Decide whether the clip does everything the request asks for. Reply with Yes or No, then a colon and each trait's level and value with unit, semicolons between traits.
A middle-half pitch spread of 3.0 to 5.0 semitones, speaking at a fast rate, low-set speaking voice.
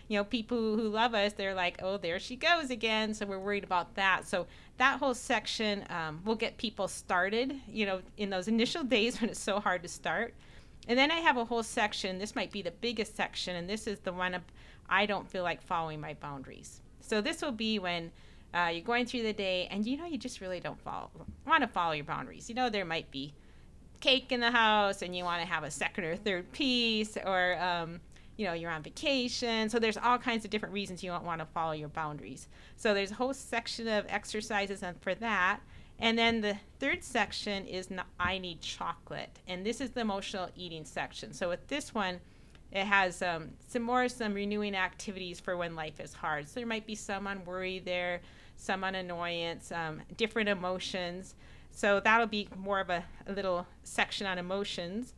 No: average, 4.2 semitones; fast, 215 wpm; high, 200 Hz